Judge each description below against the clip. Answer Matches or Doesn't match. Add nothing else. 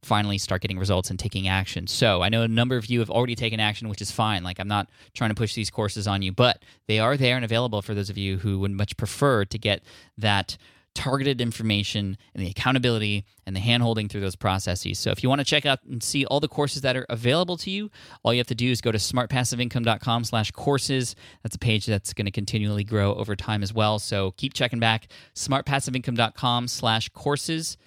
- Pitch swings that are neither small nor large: Matches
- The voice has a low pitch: Matches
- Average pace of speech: Doesn't match